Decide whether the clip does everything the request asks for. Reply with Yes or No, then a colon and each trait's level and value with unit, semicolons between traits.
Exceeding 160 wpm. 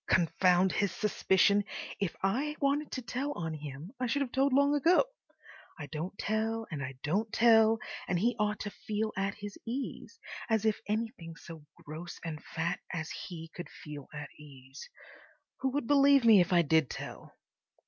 Yes: average, 175 wpm